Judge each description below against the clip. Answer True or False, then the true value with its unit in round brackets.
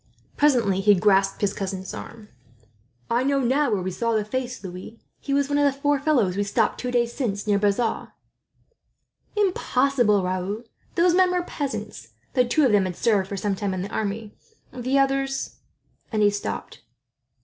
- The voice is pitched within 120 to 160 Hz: False (225 Hz)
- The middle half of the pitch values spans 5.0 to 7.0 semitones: True (5.3 semitones)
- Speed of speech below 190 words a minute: True (180 wpm)